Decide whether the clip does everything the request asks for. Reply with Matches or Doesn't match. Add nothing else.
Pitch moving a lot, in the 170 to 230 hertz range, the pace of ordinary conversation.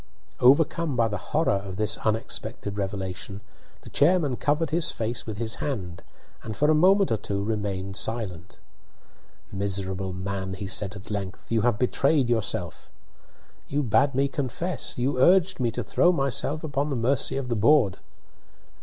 Doesn't match